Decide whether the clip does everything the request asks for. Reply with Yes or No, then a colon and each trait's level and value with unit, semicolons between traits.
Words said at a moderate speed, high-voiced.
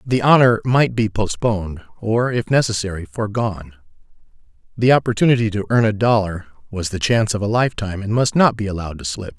No: average, 180 wpm; low, 110 Hz